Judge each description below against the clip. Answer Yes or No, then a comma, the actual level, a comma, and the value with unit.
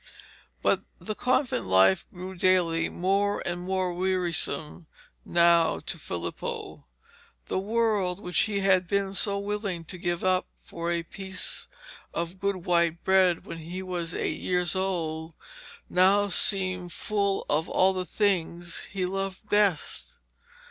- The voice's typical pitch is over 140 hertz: Yes, medium, 185 Hz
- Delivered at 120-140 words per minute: Yes, slow, 135 wpm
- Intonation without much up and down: Yes, narrow, 2.3 semitones